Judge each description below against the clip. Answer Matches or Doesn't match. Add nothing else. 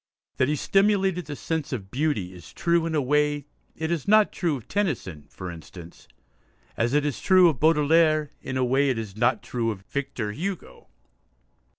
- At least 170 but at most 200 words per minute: Matches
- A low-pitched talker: Doesn't match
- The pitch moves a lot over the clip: Matches